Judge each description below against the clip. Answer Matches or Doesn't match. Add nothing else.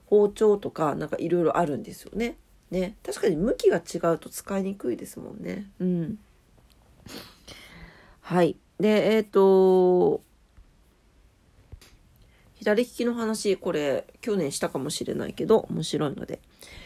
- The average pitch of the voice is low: Doesn't match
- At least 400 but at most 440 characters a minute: Doesn't match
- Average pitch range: Matches